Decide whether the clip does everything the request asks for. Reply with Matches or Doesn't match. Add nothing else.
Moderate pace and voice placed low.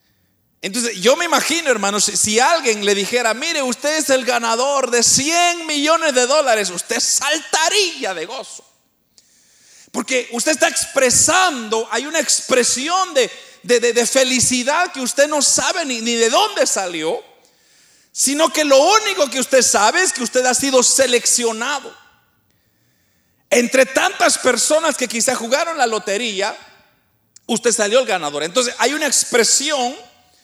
Doesn't match